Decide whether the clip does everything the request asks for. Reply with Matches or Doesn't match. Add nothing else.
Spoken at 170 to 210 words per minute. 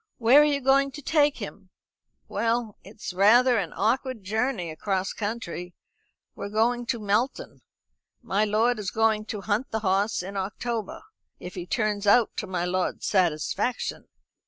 Doesn't match